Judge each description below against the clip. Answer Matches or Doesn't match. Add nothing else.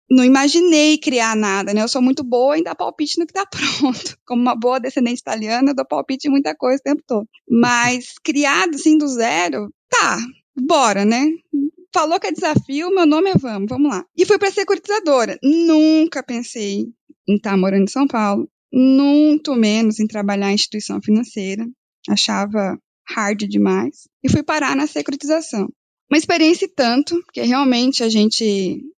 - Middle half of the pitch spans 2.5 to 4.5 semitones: Doesn't match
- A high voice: Matches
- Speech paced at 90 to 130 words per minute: Doesn't match